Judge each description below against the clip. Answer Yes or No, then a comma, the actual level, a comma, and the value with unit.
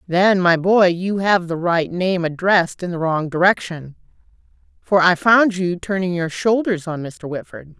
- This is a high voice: No, medium, 180 Hz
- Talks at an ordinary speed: Yes, average, 175 wpm